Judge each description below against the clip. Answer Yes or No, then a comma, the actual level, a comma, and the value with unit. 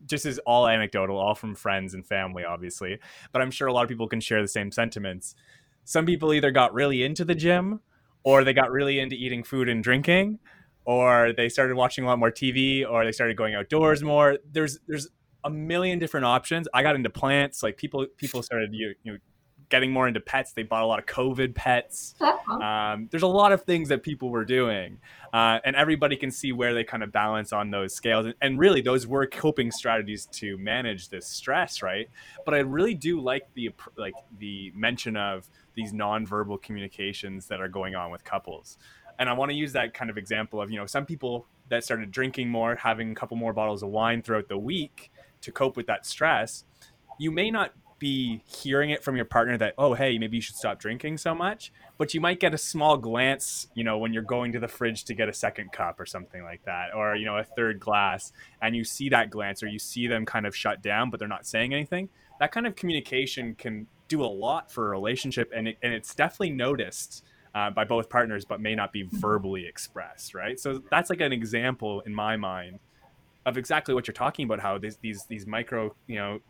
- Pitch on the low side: Yes, low, 120 Hz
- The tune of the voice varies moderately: Yes, average, 4.3 semitones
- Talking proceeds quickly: Yes, fast, 220 wpm